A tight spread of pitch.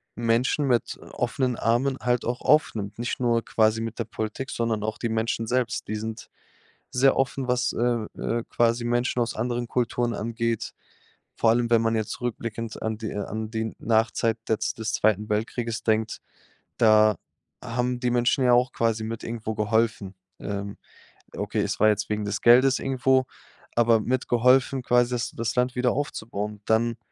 Yes: narrow, 1.9 semitones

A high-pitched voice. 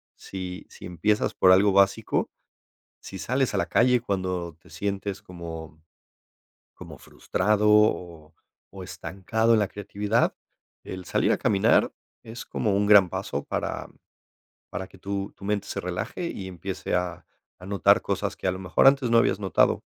No: very low, 95 Hz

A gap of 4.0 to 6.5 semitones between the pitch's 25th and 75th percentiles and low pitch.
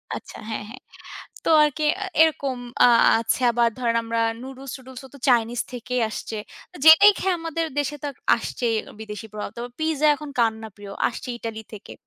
No: average, 4.5 semitones; very high, 250 Hz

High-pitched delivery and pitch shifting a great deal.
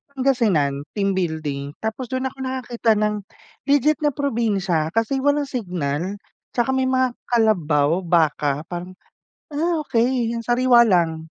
Yes: high, 220 Hz; wide, 7.5 semitones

